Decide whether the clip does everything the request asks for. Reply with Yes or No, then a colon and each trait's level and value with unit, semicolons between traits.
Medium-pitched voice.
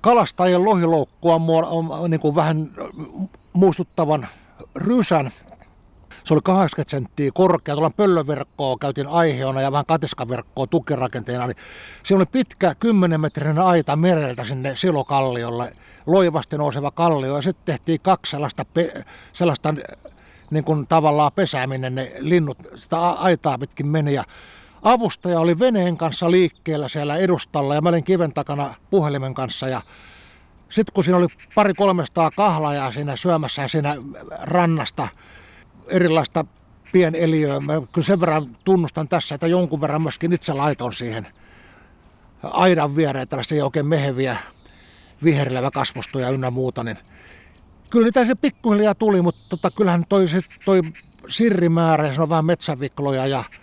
Yes: medium, 155 Hz